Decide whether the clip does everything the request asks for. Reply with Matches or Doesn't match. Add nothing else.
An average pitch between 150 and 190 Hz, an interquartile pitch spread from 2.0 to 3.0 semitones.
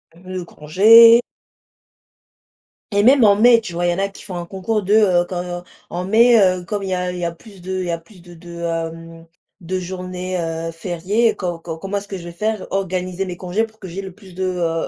Matches